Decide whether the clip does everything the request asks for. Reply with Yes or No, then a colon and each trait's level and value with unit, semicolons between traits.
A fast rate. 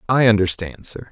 No: average, 160 wpm